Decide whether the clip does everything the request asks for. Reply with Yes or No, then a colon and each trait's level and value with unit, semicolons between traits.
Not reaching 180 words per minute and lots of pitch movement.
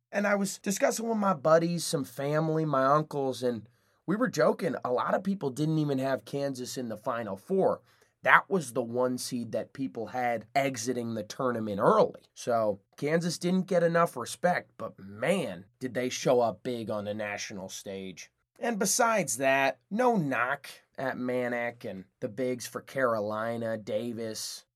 Yes: average, 165 wpm; wide, 5.9 semitones